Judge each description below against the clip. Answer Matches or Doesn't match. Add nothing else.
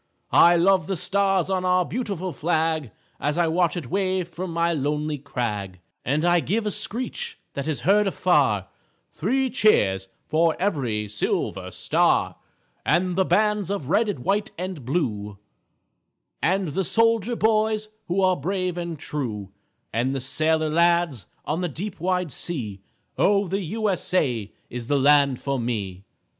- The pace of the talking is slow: Doesn't match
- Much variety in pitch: Matches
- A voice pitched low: Doesn't match